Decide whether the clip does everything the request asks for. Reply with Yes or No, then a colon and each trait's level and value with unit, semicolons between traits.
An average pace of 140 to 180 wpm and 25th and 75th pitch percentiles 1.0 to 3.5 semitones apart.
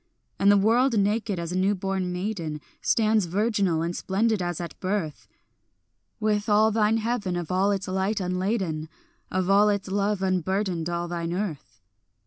Yes: average, 160 wpm; average, 3.1 semitones